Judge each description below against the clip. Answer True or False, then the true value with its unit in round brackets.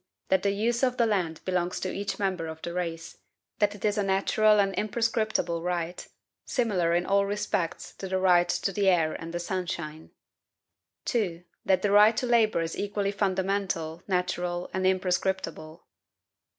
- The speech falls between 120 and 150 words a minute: False (165 wpm)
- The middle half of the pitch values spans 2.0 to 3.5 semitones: True (2.8 semitones)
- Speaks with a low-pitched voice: False (190 Hz)